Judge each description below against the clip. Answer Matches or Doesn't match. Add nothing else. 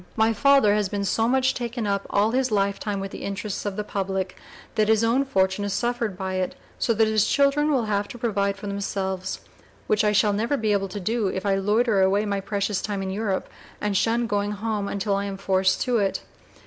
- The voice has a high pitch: Matches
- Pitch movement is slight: Matches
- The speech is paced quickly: Matches